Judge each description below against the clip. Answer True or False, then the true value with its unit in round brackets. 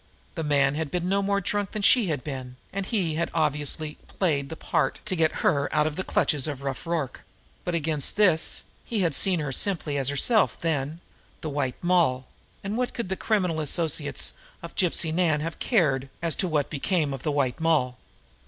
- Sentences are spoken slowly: False (200 wpm)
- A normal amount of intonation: True (4.3 semitones)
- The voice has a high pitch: False (160 Hz)